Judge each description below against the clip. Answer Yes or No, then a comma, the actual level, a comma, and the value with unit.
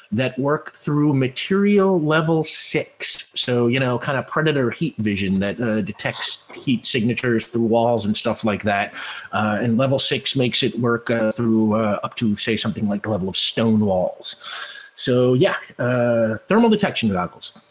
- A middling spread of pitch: Yes, average, 3.7 semitones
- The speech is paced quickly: No, average, 175 wpm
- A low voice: Yes, low, 120 Hz